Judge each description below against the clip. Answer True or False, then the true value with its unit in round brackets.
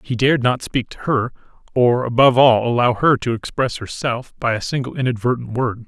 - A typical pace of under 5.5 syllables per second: False (5.7 syllables/s)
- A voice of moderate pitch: False (120 Hz)